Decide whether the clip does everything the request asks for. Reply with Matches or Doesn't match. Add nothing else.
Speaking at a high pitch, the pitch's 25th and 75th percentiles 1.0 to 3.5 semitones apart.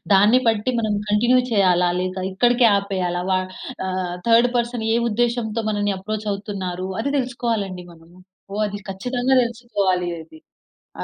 Doesn't match